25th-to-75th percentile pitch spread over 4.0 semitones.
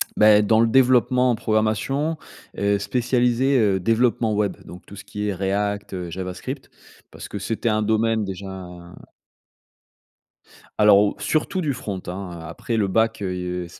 No: average, 3.1 semitones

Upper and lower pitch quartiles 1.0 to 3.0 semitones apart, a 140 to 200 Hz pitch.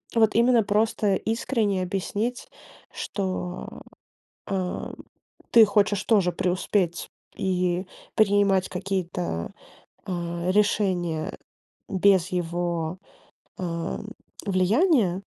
Yes: average, 2.7 semitones; high, 190 Hz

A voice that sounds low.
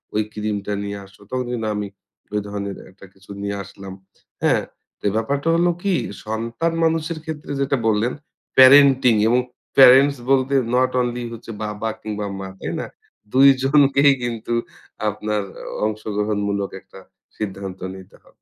Yes: low, 115 Hz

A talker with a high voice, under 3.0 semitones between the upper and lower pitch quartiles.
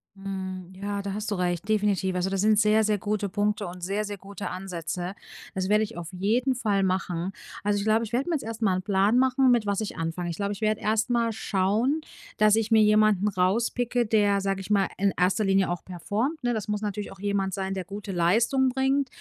Yes: high, 205 Hz; narrow, 2.4 semitones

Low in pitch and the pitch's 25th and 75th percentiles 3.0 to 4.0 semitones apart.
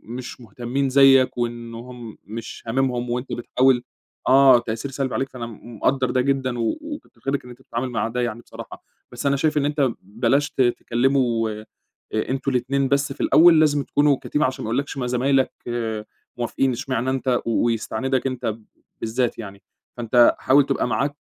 No: low, 130 Hz; narrow, 2.4 semitones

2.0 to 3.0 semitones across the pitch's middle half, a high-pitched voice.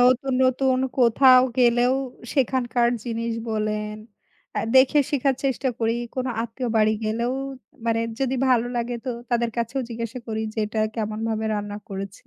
Yes: narrow, 2.5 semitones; high, 235 Hz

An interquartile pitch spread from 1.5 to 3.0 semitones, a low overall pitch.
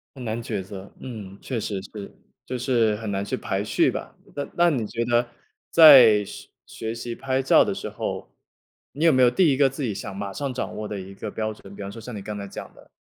No: average, 4.2 semitones; low, 110 Hz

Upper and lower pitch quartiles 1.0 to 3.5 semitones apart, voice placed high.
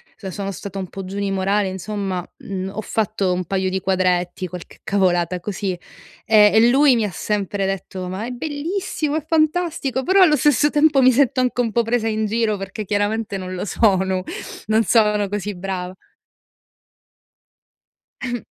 No: average, 4.2 semitones; high, 205 Hz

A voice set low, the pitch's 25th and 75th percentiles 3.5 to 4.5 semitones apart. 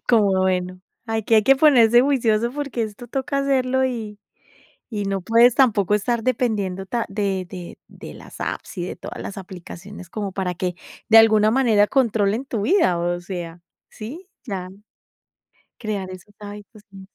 No: high, 215 Hz; average, 4.0 semitones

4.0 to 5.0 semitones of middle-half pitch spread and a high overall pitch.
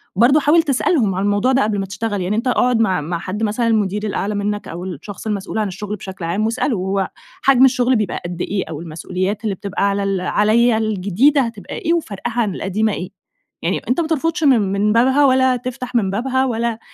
Yes: average, 4.3 semitones; high, 210 Hz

